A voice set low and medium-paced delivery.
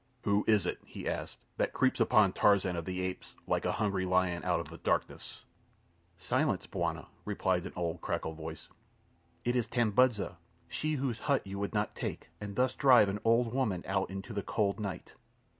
Yes: low, 100 Hz; average, 180 wpm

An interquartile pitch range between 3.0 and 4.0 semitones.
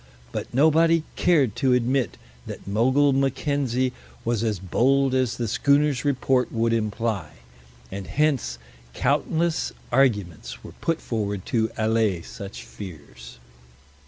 No: average, 4.5 semitones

